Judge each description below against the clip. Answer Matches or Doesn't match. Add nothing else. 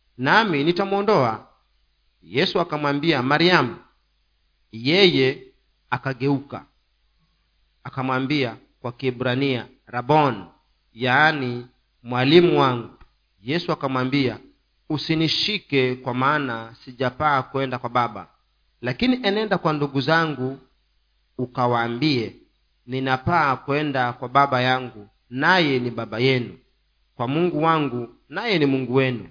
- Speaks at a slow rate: Matches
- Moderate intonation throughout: Matches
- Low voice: Matches